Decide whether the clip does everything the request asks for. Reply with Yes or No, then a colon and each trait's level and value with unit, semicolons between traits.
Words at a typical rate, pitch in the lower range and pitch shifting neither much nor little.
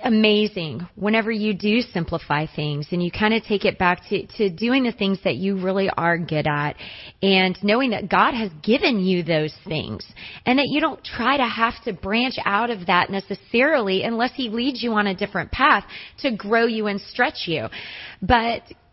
No: average, 195 wpm; high, 205 Hz; average, 4.4 semitones